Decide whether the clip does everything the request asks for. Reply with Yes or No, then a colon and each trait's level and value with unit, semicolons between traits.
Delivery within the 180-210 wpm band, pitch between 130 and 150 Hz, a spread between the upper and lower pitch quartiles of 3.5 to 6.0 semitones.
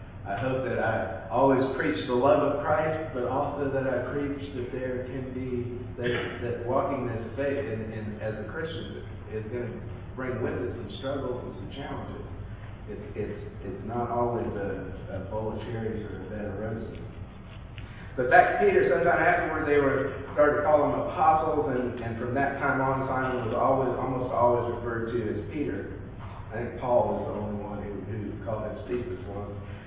No: average, 185 wpm; low, 115 Hz; average, 3.9 semitones